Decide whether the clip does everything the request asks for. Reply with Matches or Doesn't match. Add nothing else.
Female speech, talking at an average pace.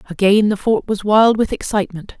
Matches